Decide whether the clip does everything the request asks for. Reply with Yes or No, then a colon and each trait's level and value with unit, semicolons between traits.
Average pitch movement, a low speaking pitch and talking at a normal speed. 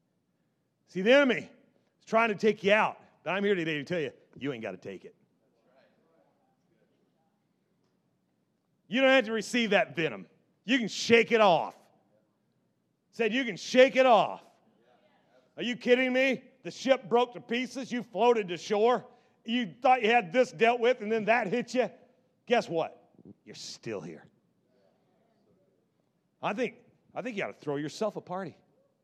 No: average, 3.8 semitones; high, 230 Hz; average, 165 wpm